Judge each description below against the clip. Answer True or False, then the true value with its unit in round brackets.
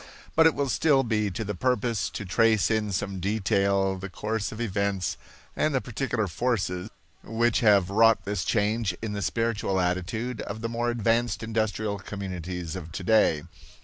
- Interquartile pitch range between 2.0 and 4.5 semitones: True (3.2 semitones)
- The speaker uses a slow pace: False (165 wpm)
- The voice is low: True (105 Hz)